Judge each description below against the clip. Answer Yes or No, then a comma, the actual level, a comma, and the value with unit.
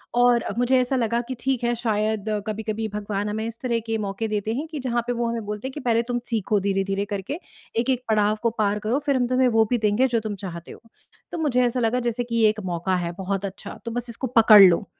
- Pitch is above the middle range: Yes, high, 225 Hz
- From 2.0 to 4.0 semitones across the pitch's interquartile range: Yes, average, 2.8 semitones